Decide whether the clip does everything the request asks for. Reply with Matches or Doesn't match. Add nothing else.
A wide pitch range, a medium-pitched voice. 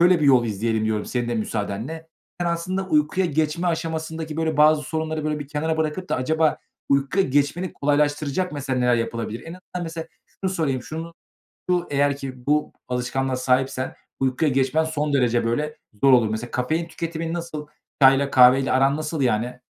Doesn't match